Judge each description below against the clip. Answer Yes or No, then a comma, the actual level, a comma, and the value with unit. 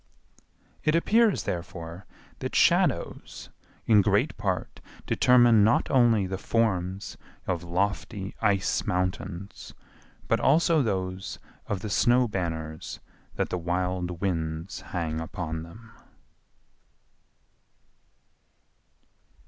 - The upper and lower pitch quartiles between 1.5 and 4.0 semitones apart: No, average, 4.5 semitones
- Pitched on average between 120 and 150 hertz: No, very low, 95 Hz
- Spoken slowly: Yes, slow, 95 wpm